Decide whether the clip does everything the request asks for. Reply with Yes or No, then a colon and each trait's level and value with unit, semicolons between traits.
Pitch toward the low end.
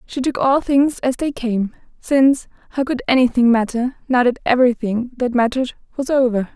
No: very high, 250 Hz